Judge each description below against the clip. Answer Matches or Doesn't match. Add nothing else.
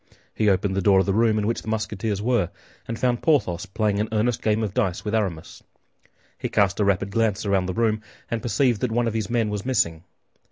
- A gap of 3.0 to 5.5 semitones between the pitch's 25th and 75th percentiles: Doesn't match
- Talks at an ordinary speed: Doesn't match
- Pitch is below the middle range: Matches